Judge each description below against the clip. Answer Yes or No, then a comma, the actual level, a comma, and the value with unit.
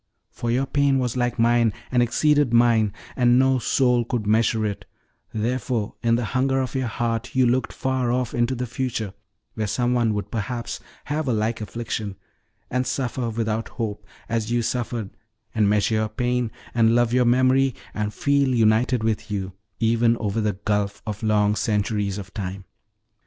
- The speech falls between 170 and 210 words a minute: Yes, average, 175 wpm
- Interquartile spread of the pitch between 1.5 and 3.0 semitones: Yes, narrow, 2.6 semitones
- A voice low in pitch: Yes, low, 115 Hz